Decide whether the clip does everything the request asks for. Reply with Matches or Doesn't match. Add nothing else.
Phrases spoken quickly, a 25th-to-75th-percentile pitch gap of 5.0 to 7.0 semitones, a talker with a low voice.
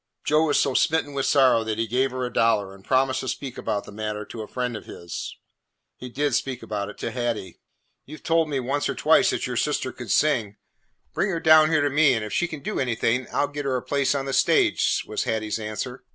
Doesn't match